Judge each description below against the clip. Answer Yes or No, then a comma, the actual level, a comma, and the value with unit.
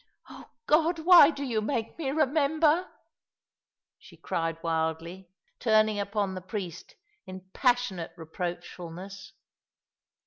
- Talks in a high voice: Yes, high, 205 Hz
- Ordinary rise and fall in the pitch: No, wide, 8.2 semitones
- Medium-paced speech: No, slow, 105 wpm